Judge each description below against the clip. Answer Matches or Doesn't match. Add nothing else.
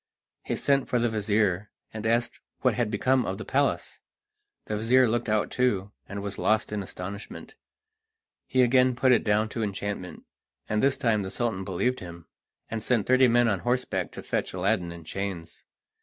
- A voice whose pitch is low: Matches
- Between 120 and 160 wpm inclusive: Doesn't match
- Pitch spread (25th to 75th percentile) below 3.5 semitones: Doesn't match